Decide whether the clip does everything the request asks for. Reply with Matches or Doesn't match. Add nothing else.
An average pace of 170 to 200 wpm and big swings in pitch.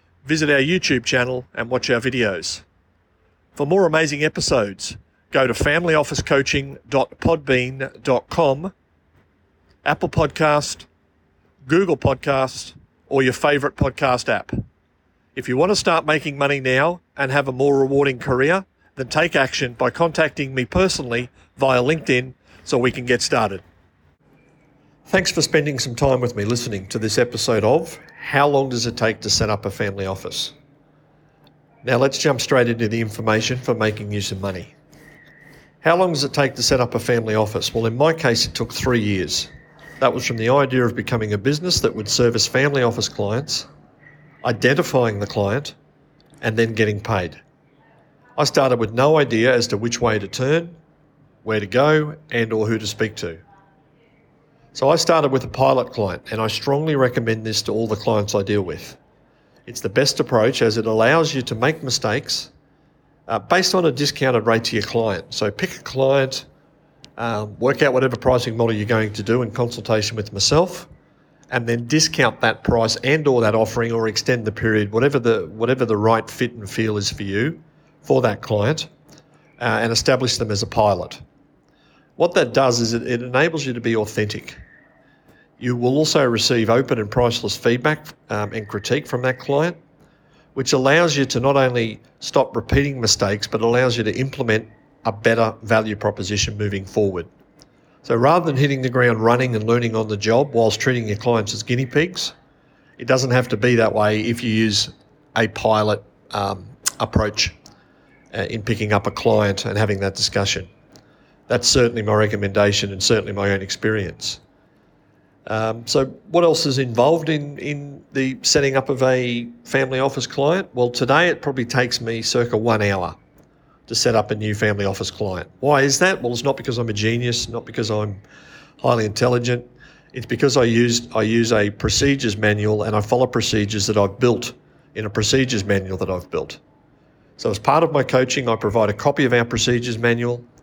Doesn't match